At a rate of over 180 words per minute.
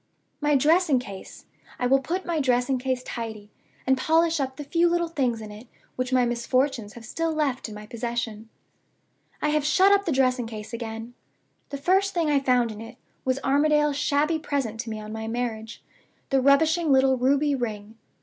Yes: average, 190 wpm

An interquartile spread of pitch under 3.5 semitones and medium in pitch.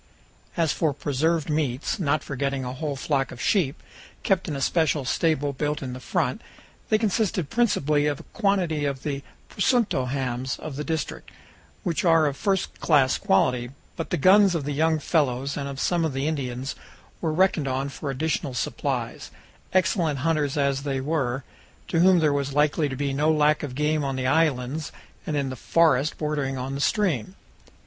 Yes: average, 3.1 semitones; medium, 145 Hz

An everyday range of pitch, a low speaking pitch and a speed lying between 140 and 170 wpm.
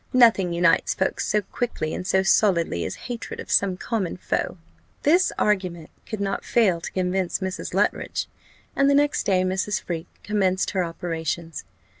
No: average, 3.4 semitones; high, 190 Hz; average, 160 wpm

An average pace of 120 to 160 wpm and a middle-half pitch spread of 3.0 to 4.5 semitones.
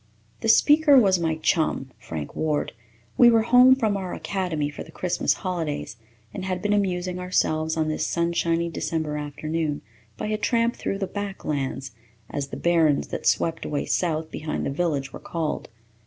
No: average, 170 wpm; average, 4.1 semitones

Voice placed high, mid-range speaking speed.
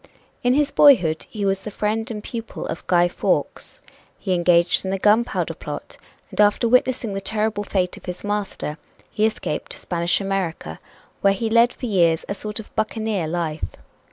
Yes: high, 205 Hz; average, 180 wpm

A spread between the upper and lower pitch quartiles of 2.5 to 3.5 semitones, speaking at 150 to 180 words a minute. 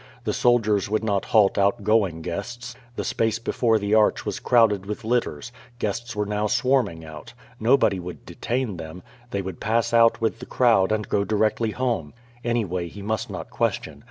Yes: average, 3.0 semitones; average, 175 wpm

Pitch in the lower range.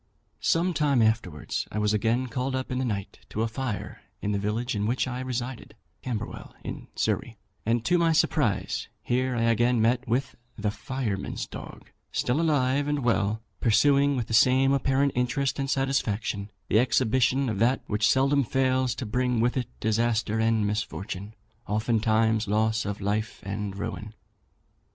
Yes: low, 120 Hz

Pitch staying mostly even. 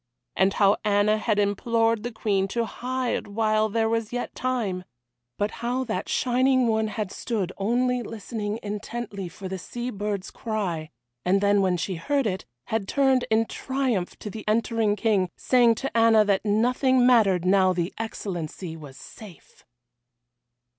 No: average, 3.3 semitones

